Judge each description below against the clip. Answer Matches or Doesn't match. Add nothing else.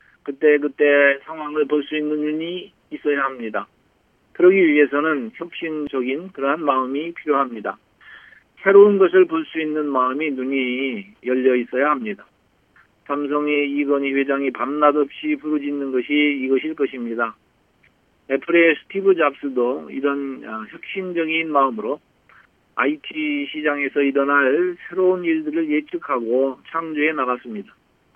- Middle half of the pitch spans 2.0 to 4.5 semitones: Matches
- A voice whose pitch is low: Doesn't match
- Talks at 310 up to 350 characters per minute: Doesn't match